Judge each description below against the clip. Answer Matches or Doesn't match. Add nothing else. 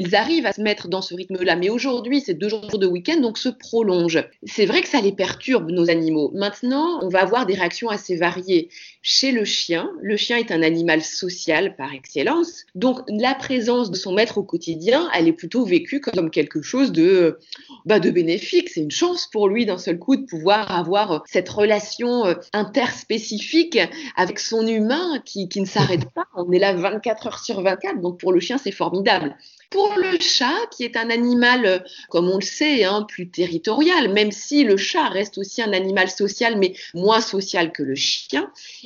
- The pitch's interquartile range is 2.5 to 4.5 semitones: Doesn't match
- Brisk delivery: Doesn't match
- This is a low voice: Doesn't match